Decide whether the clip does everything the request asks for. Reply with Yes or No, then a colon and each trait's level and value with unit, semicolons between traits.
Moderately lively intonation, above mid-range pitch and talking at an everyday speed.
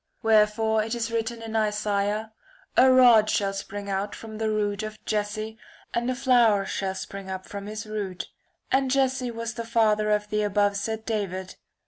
No: narrow, 1.9 semitones; high, 215 Hz; average, 180 wpm